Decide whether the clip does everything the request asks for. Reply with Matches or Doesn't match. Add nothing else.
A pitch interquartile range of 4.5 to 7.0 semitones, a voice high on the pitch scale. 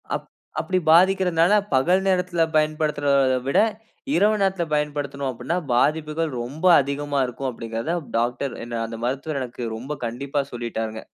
Doesn't match